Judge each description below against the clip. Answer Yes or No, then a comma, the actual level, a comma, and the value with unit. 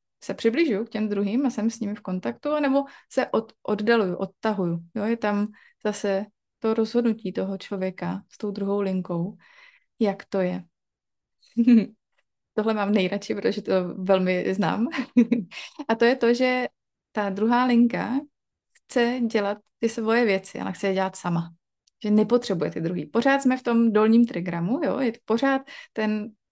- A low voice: No, high, 215 Hz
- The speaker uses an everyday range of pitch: Yes, average, 3.6 semitones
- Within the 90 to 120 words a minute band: No, average, 160 wpm